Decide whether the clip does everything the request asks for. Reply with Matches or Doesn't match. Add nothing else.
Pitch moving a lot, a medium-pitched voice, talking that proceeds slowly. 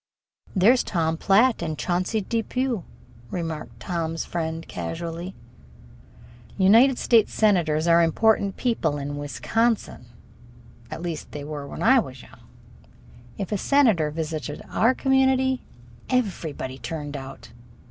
Matches